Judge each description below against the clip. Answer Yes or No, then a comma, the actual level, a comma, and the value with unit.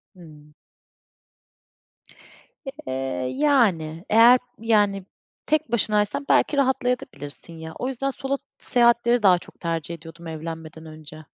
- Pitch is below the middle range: No, high, 195 Hz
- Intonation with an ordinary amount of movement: No, wide, 7.4 semitones